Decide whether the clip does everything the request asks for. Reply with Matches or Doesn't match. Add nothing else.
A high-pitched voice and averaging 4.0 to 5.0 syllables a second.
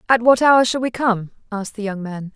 Doesn't match